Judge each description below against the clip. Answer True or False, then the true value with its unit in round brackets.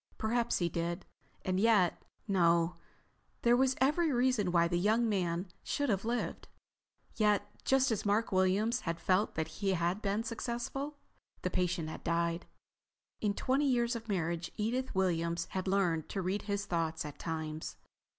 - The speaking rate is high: False (155 wpm)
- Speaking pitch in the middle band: False (195 Hz)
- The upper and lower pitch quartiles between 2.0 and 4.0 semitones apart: False (5.2 semitones)